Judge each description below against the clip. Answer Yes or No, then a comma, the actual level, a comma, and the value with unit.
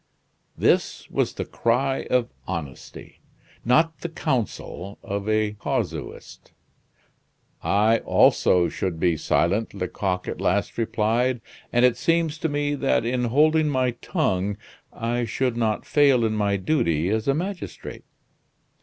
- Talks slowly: Yes, slow, 130 wpm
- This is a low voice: Yes, low, 115 Hz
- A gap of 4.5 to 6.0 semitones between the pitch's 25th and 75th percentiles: Yes, wide, 5.4 semitones